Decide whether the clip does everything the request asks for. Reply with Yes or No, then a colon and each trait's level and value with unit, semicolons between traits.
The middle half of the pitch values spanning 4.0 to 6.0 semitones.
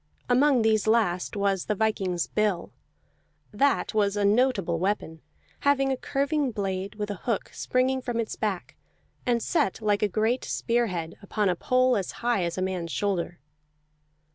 Yes: average, 4.3 semitones